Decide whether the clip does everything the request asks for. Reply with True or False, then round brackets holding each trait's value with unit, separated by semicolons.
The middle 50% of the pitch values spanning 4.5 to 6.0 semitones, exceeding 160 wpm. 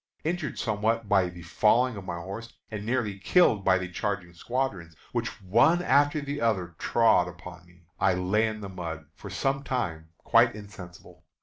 True (4.8 semitones; 175 wpm)